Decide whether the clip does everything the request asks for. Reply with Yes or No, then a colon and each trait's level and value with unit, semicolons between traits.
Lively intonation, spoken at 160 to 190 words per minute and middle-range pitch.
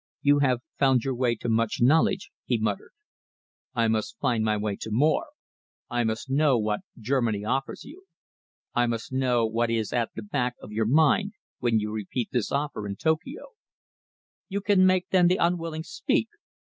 No: wide, 5.7 semitones; average, 175 wpm; low, 125 Hz